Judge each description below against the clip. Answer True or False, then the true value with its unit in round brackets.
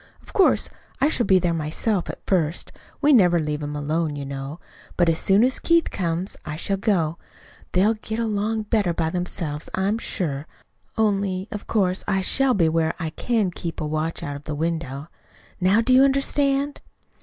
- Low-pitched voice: False (180 Hz)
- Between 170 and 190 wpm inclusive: True (180 wpm)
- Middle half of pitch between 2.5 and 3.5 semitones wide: False (5.4 semitones)